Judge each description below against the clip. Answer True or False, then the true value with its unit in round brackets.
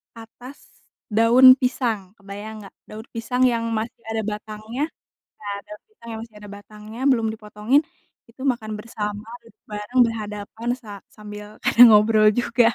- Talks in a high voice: True (220 Hz)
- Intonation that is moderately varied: False (1.9 semitones)